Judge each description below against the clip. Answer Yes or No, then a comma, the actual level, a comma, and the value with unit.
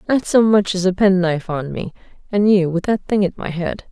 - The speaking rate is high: Yes, fast, 245 wpm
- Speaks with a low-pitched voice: No, high, 190 Hz